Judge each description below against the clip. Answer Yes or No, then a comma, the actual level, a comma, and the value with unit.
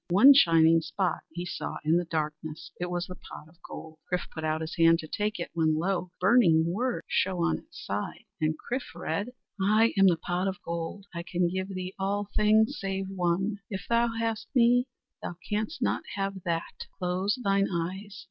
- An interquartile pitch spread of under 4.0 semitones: Yes, average, 3.4 semitones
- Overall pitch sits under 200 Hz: Yes, medium, 185 Hz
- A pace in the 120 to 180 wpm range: No, average, 195 wpm